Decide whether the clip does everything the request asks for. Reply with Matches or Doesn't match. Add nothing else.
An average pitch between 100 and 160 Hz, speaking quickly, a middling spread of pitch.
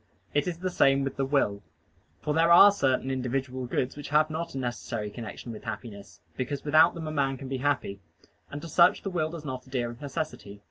Matches